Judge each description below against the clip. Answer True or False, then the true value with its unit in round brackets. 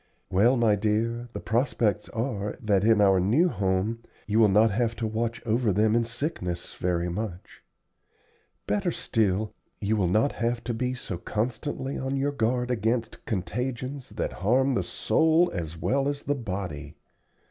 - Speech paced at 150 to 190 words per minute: True (160 wpm)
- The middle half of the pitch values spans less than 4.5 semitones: True (3.8 semitones)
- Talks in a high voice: False (115 Hz)